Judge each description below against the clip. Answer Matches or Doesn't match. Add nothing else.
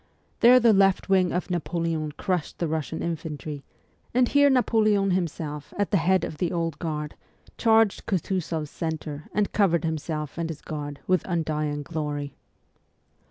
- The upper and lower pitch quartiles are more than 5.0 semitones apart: Doesn't match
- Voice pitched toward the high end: Doesn't match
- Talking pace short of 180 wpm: Matches